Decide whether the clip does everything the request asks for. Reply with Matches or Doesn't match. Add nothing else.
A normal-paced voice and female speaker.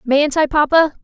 Matches